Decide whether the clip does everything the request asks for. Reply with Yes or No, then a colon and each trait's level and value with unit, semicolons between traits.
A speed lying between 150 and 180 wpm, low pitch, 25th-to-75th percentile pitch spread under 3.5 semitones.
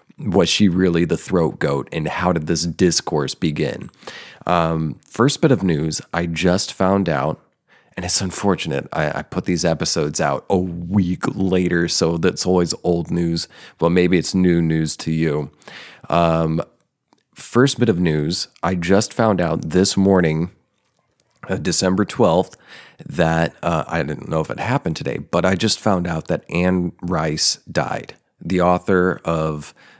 Yes: average, 160 wpm; very low, 90 Hz; narrow, 2.4 semitones